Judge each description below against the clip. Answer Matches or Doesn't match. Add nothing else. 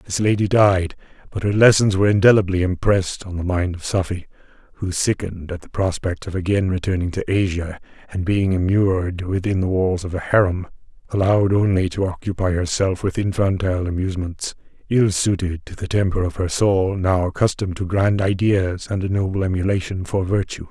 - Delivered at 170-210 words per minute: Matches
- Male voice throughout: Matches